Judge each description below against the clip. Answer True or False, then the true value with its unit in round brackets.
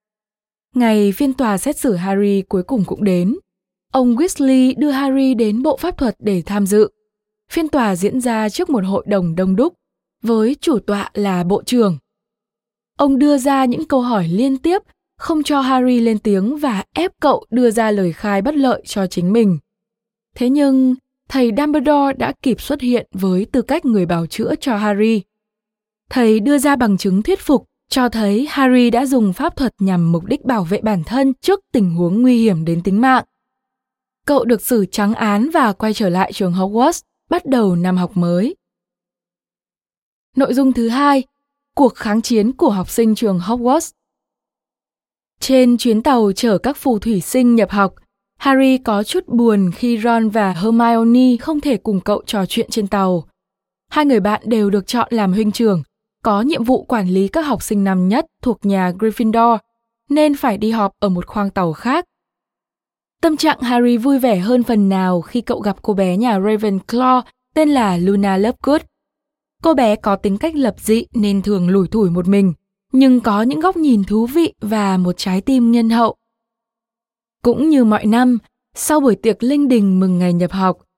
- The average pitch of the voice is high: True (230 Hz)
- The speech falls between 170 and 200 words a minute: True (185 wpm)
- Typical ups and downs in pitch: True (4.4 semitones)